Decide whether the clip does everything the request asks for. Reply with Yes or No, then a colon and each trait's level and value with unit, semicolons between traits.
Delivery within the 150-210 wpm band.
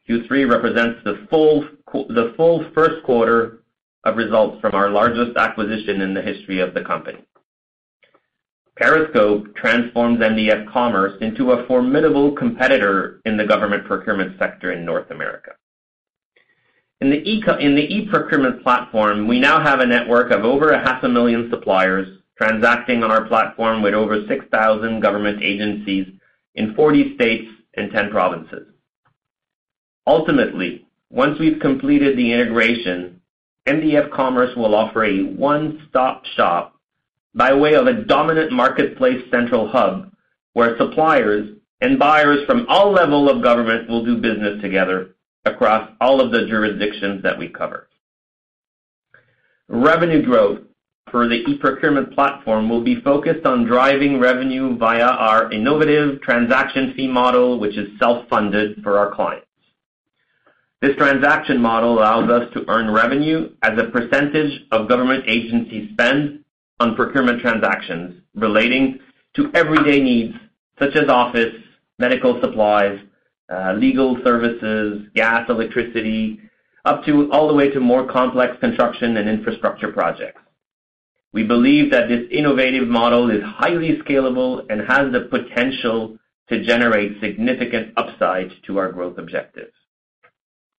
No: slow, 135 wpm